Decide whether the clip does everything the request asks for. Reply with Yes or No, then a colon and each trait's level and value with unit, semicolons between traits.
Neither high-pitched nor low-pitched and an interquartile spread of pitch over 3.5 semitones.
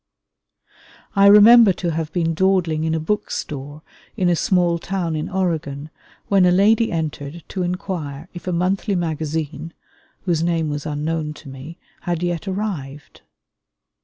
No: medium, 170 Hz; average, 3.2 semitones